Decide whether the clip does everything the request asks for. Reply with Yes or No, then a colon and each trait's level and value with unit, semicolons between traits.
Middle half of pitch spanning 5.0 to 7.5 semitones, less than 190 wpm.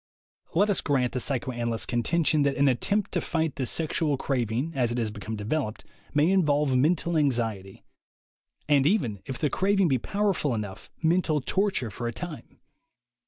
Yes: wide, 5.5 semitones; average, 165 wpm